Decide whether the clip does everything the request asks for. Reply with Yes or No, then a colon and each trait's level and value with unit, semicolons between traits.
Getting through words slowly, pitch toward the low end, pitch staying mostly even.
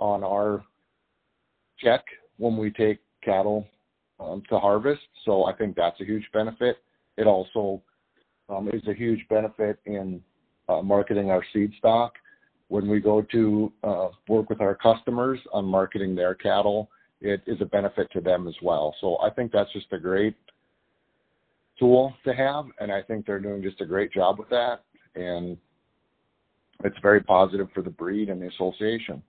No: average, 170 wpm; low, 105 Hz; narrow, 2.1 semitones